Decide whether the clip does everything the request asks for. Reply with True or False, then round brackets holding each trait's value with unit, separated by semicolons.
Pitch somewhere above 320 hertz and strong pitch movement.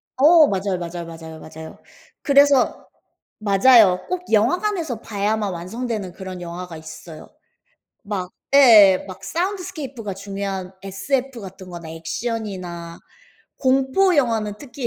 False (205 Hz; 6.3 semitones)